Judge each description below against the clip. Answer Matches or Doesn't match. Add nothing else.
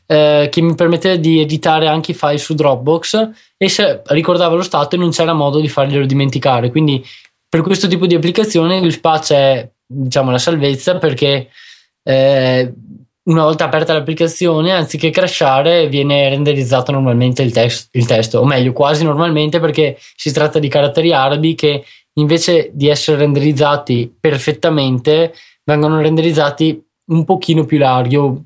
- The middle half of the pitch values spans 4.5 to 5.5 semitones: Doesn't match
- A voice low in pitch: Doesn't match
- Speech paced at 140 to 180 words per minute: Matches